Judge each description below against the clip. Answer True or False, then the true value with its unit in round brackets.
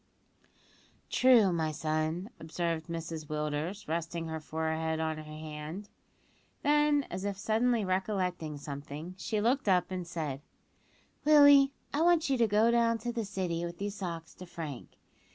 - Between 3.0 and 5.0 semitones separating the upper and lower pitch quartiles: False (5.6 semitones)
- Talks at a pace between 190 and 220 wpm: False (150 wpm)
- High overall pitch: False (175 Hz)